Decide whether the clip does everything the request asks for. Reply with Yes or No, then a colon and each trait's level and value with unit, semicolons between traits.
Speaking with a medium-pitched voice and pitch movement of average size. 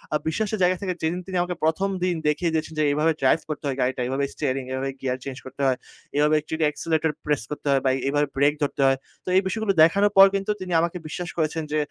Yes: medium, 155 Hz; average, 4.2 semitones